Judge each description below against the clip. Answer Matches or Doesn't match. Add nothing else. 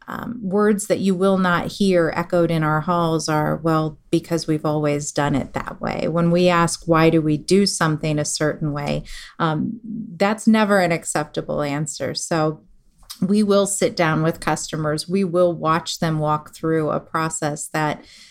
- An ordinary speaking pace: Matches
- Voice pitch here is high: Doesn't match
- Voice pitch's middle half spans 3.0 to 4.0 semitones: Matches